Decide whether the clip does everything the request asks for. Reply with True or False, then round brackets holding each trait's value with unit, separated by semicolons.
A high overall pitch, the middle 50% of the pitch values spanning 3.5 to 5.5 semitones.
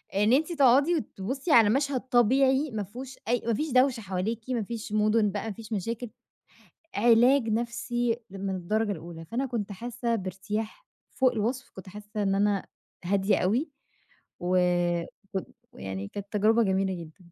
True (220 Hz; 4.0 semitones)